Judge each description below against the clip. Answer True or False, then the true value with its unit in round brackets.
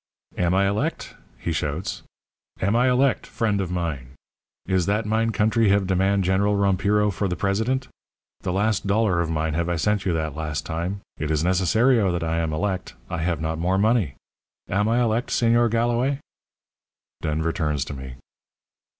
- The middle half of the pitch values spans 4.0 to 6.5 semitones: True (4.6 semitones)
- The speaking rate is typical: True (175 wpm)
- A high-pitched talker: False (95 Hz)